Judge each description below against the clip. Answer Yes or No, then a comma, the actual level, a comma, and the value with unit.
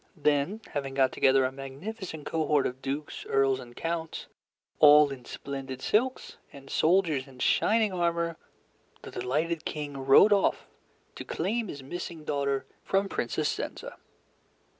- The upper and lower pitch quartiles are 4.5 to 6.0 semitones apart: No, average, 4.1 semitones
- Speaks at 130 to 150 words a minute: Yes, average, 140 wpm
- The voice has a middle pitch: Yes, medium, 150 Hz